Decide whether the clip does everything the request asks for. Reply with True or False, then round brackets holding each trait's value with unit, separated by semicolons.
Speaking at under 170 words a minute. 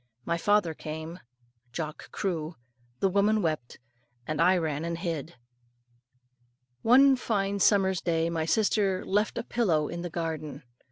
True (135 wpm)